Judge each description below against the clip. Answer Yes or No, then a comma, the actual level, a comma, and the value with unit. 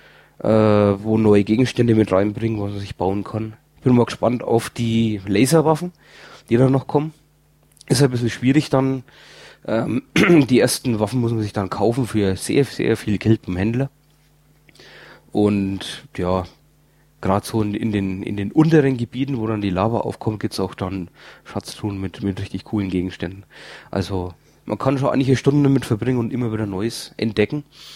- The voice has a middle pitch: No, low, 110 Hz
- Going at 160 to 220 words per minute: Yes, average, 180 wpm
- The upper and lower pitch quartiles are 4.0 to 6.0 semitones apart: Yes, average, 4.7 semitones